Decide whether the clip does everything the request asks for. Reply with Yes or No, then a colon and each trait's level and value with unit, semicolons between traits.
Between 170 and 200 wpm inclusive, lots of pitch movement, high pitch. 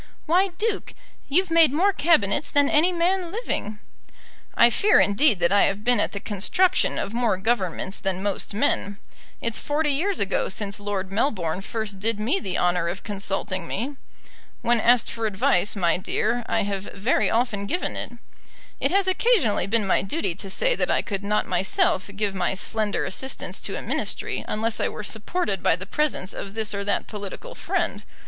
Yes: average, 180 wpm; wide, 6.9 semitones; high, 215 Hz